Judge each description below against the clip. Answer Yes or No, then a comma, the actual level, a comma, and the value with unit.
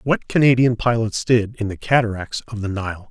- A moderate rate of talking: Yes, average, 195 wpm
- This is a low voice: Yes, low, 115 Hz